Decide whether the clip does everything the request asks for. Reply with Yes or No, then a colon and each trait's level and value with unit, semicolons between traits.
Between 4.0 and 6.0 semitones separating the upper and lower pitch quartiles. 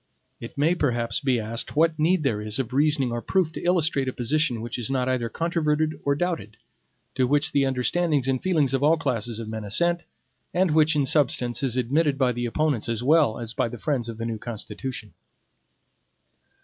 Yes: average, 4.7 semitones